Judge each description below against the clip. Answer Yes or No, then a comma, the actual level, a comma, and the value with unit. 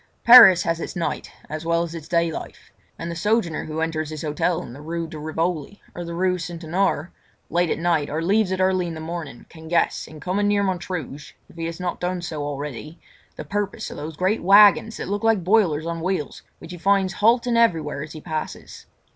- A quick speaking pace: Yes, fast, 215 wpm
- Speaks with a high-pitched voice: No, medium, 170 Hz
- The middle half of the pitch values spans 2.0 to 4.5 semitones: Yes, average, 3.0 semitones